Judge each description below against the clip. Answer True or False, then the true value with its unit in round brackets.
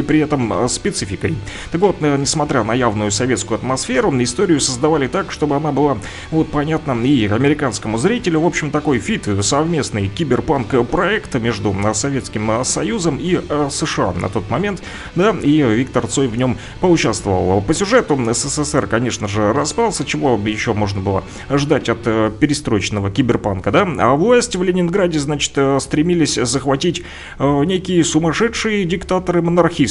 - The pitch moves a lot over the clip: True (6.1 semitones)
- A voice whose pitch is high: False (140 Hz)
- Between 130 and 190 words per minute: True (140 wpm)